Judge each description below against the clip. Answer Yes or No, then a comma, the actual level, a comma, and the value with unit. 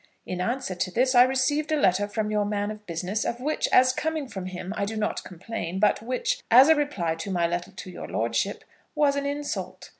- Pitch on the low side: No, high, 215 Hz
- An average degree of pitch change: No, wide, 6.1 semitones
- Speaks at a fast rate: Yes, fast, 220 wpm